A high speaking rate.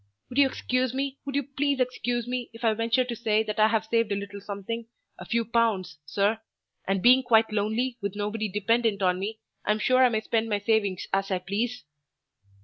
Yes: fast, 210 wpm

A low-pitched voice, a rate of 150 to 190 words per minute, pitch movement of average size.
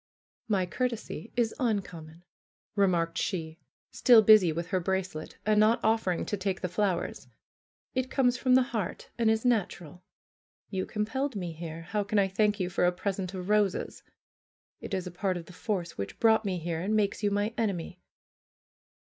No: high, 195 Hz; average, 175 wpm; average, 3.6 semitones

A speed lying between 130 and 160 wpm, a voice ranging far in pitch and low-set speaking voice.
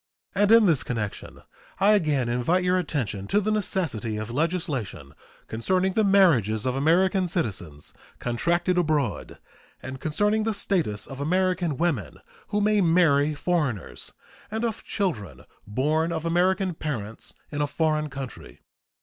No: average, 140 wpm; wide, 6.9 semitones; medium, 160 Hz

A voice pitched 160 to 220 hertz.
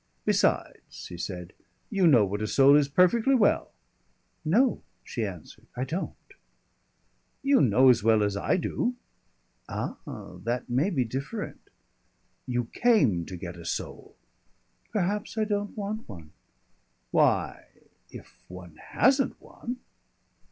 No: low, 135 Hz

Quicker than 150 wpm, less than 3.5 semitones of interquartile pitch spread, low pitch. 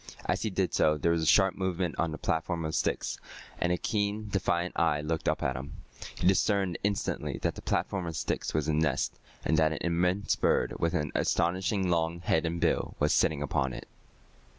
Yes: fast, 205 wpm; average, 3.1 semitones; very low, 85 Hz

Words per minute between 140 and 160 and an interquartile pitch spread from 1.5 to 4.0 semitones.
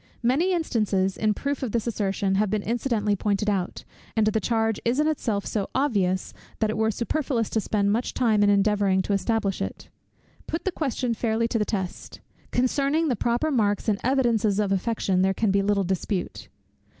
No: average, 185 wpm; average, 3.2 semitones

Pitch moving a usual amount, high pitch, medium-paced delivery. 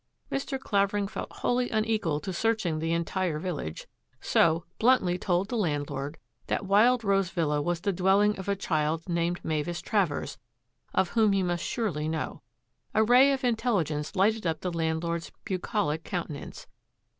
No: average, 4.6 semitones; medium, 180 Hz; average, 160 wpm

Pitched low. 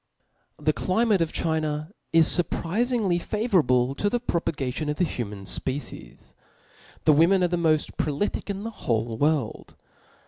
No: medium, 160 Hz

